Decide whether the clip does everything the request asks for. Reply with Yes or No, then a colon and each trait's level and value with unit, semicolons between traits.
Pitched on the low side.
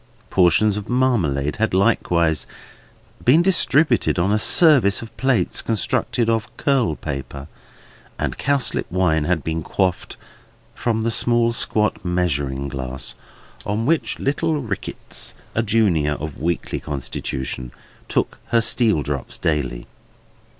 Yes: very low, 95 Hz